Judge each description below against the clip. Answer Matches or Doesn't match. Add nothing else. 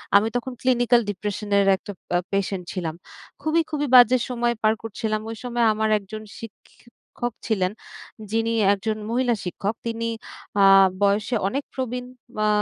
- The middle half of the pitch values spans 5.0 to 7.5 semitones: Doesn't match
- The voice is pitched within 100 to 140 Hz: Doesn't match